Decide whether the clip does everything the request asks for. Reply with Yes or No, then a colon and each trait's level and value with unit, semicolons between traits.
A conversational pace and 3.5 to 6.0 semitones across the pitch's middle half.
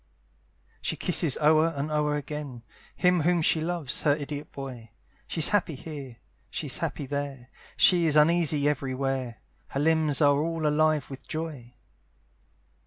No: average, 145 wpm; narrow, 2.5 semitones